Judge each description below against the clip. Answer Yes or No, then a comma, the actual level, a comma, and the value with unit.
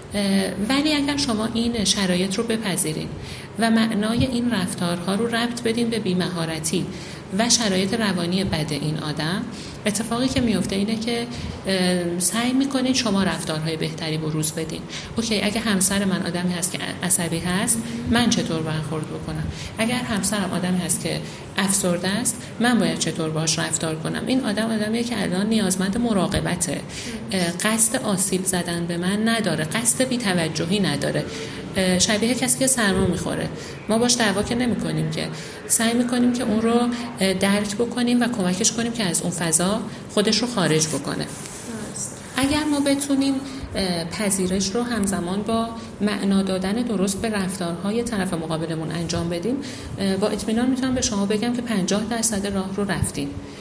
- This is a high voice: Yes, high, 200 Hz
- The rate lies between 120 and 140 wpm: No, average, 150 wpm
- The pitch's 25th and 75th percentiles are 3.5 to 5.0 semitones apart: Yes, average, 4.5 semitones